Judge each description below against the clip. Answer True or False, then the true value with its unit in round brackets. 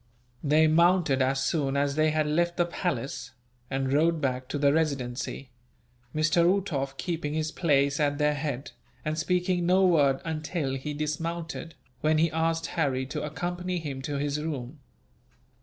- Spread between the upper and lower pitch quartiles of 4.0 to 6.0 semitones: False (3.0 semitones)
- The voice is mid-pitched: True (155 Hz)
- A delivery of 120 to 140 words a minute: False (155 wpm)